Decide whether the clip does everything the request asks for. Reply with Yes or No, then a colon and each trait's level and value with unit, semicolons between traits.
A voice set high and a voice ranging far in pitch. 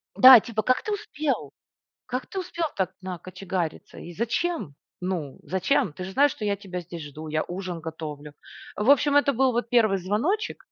Yes: high, 200 Hz; wide, 7.2 semitones